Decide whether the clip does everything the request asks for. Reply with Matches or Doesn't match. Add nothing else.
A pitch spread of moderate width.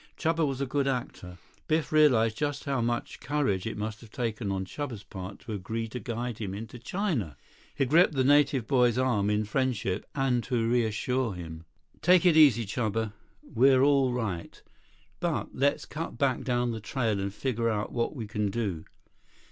Matches